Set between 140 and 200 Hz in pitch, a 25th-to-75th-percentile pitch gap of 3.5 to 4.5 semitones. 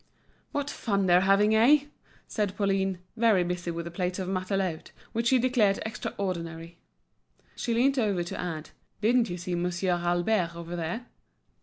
Yes: high, 190 Hz; average, 3.9 semitones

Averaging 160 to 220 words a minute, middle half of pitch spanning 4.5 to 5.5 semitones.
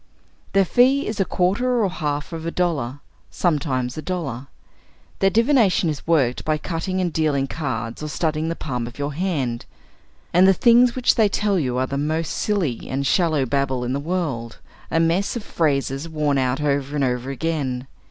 Yes: average, 185 wpm; average, 5.2 semitones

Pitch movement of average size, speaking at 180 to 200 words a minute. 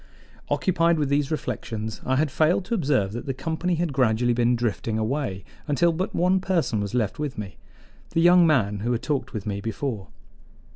No: wide, 6.7 semitones; average, 190 wpm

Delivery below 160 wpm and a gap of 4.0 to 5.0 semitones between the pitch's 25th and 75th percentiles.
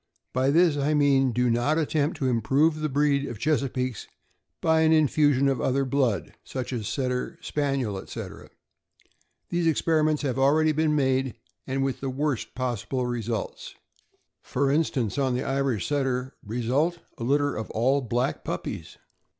No: average, 150 wpm; average, 2.8 semitones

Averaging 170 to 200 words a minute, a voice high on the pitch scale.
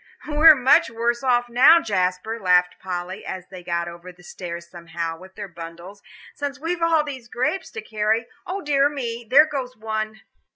Yes: average, 180 wpm; high, 220 Hz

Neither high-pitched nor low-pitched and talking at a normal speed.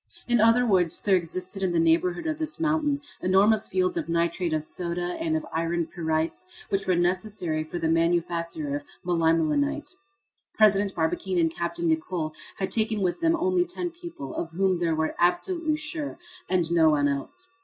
Yes: medium, 180 Hz; average, 175 wpm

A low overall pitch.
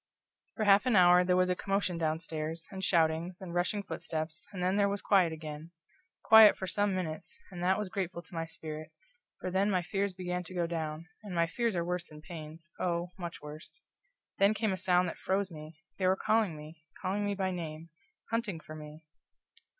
No: medium, 180 Hz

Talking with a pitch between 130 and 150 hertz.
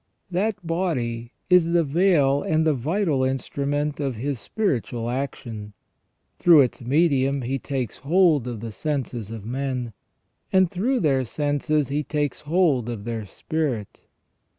Yes: medium, 140 Hz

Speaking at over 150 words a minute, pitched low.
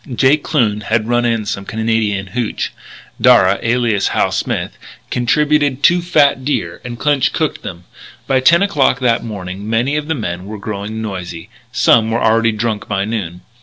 Yes: average, 165 wpm; low, 115 Hz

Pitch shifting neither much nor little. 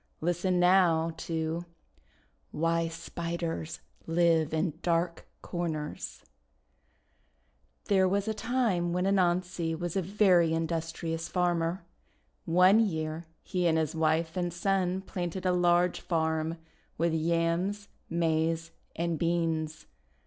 No: narrow, 1.8 semitones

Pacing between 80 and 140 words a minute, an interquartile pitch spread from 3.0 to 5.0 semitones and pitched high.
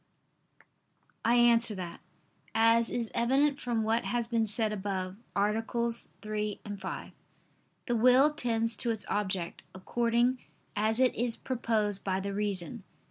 No: slow, 135 wpm; narrow, 2.5 semitones; high, 225 Hz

